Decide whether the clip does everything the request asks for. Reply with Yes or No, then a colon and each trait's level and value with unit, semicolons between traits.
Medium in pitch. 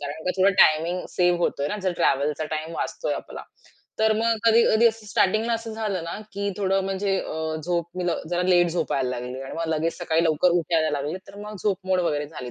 Yes: medium, 175 Hz